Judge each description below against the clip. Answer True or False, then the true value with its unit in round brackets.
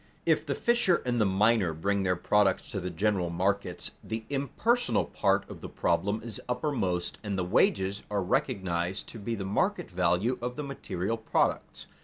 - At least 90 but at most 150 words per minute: False (175 wpm)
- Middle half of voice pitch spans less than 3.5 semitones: False (4.0 semitones)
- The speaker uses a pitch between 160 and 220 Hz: False (100 Hz)